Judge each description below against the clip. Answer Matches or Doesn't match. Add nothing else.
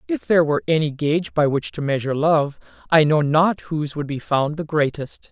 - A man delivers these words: Doesn't match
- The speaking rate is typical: Doesn't match